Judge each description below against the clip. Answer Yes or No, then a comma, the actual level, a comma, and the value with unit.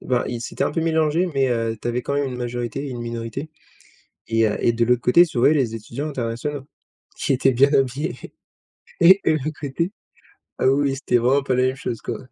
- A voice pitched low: Yes, low, 130 Hz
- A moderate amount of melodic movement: Yes, average, 3.3 semitones